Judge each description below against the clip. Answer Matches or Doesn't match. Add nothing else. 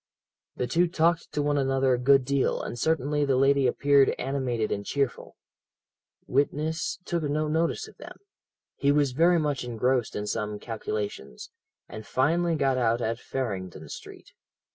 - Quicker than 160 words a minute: Doesn't match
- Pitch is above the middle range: Doesn't match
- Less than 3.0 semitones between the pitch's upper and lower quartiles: Doesn't match